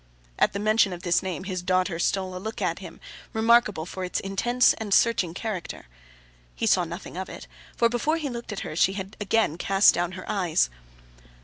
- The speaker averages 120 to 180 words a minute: No, average, 200 wpm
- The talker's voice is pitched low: No, high, 195 Hz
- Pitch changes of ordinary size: Yes, average, 3.6 semitones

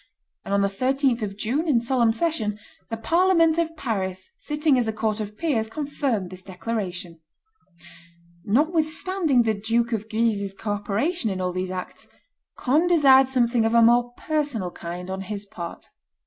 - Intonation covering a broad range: Yes, wide, 5.9 semitones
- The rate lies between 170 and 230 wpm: No, average, 160 wpm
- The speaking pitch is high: Yes, high, 230 Hz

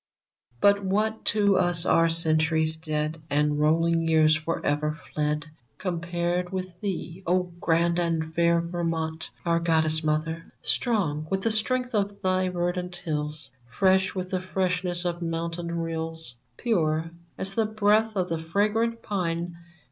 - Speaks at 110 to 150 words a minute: Yes, average, 140 wpm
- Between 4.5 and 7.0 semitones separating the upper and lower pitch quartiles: No, average, 2.7 semitones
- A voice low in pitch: No, medium, 170 Hz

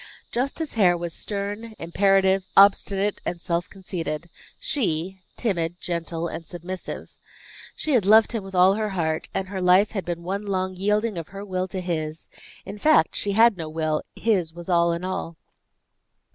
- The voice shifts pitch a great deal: No, average, 3.0 semitones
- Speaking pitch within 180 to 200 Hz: Yes, medium, 185 Hz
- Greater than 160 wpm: Yes, average, 170 wpm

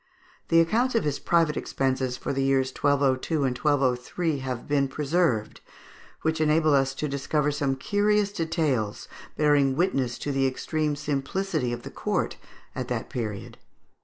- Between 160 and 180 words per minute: No, average, 150 wpm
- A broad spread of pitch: No, average, 3.2 semitones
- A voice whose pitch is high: No, medium, 145 Hz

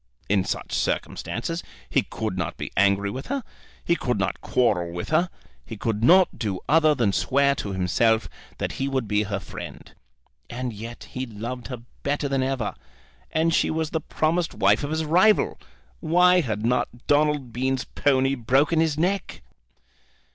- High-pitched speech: No, low, 130 Hz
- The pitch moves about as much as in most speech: No, wide, 6.1 semitones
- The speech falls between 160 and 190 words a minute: Yes, average, 170 wpm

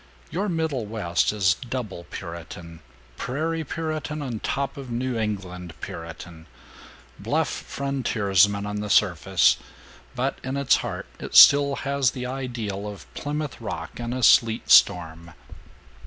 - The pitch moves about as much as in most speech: No, wide, 6.8 semitones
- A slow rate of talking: Yes, slow, 125 wpm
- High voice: No, low, 115 Hz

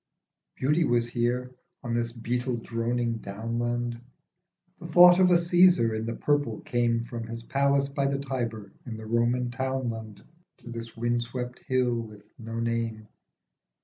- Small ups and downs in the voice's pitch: Yes, narrow, 2.3 semitones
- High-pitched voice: No, low, 120 Hz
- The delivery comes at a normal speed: Yes, average, 150 wpm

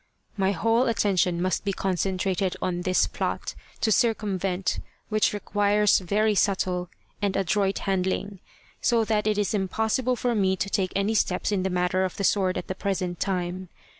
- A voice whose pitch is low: No, high, 195 Hz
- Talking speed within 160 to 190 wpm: Yes, average, 165 wpm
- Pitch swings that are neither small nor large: No, narrow, 2.2 semitones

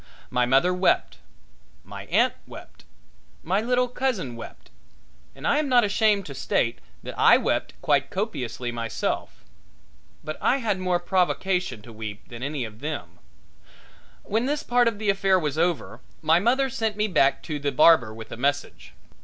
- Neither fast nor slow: Yes, average, 165 wpm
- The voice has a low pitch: No, medium, 175 Hz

